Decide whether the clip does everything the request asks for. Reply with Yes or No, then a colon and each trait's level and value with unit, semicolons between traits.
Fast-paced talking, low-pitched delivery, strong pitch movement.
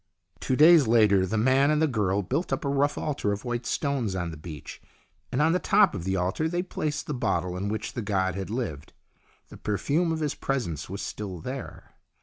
Yes: fast, 215 wpm; low, 115 Hz; wide, 7.2 semitones